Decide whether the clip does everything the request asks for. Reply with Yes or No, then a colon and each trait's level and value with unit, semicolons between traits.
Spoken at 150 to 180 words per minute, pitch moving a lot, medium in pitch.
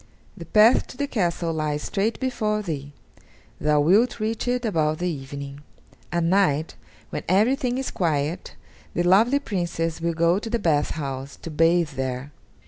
Yes: average, 160 wpm; wide, 6.0 semitones; medium, 170 Hz